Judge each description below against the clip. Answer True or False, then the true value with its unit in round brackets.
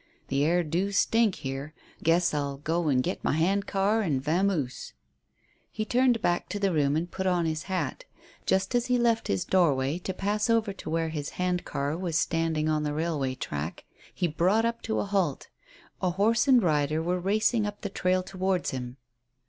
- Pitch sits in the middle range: True (175 Hz)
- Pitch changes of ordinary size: True (4.7 semitones)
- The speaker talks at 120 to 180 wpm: False (195 wpm)